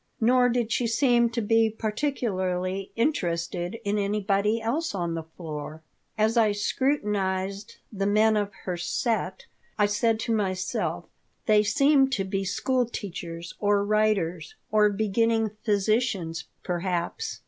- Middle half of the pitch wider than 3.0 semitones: Yes, average, 3.4 semitones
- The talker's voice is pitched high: Yes, high, 210 Hz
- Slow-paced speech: Yes, slow, 130 wpm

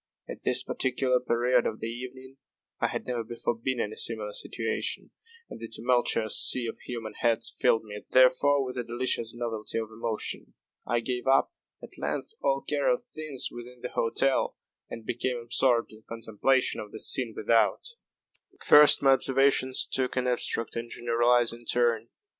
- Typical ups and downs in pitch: No, narrow, 2.1 semitones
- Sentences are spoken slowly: No, average, 170 wpm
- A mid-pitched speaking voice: No, low, 120 Hz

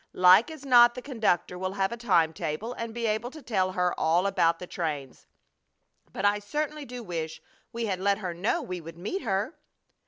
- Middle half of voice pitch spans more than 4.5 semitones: Yes, average, 5.0 semitones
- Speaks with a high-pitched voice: Yes, high, 200 Hz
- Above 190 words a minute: Yes, fast, 205 wpm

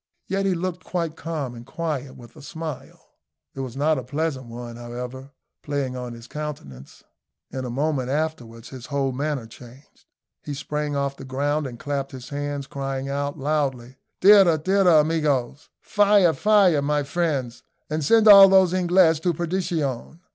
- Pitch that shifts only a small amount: No, average, 3.9 semitones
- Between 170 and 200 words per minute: No, average, 160 wpm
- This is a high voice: No, medium, 145 Hz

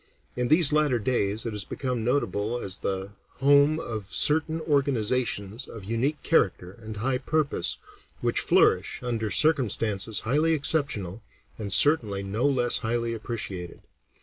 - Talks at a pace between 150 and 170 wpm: No, slow, 135 wpm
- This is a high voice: No, low, 120 Hz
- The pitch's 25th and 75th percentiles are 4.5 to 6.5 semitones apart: Yes, wide, 5.4 semitones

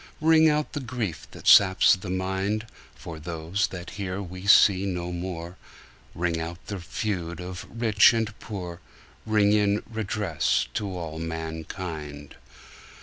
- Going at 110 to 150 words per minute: Yes, average, 140 wpm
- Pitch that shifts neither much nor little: Yes, average, 3.6 semitones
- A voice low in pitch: Yes, very low, 95 Hz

